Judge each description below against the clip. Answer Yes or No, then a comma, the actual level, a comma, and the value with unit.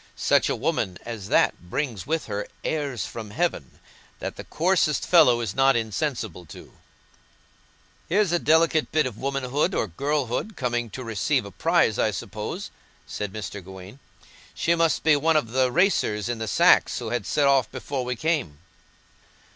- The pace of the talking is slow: No, average, 165 wpm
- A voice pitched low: Yes, low, 130 Hz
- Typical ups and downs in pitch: No, wide, 5.9 semitones